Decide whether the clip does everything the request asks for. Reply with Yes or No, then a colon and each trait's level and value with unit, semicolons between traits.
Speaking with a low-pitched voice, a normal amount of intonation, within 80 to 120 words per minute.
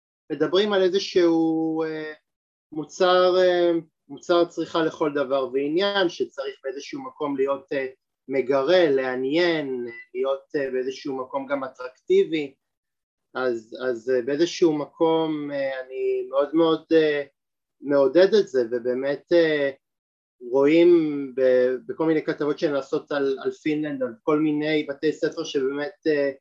No: medium, 150 Hz; average, 3.9 semitones; slow, 100 wpm